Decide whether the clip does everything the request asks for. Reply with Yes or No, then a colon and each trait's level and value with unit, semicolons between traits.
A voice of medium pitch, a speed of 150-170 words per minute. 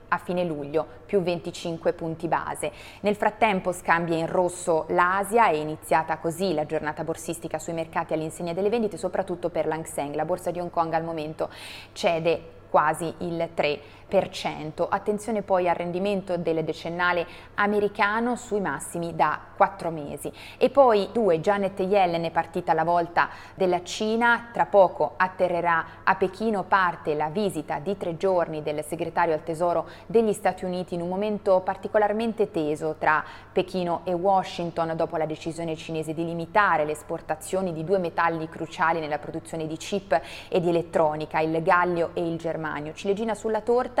Yes: medium, 170 Hz; average, 160 wpm